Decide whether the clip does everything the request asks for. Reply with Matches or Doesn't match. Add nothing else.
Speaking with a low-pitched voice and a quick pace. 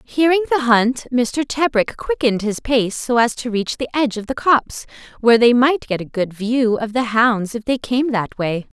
Doesn't match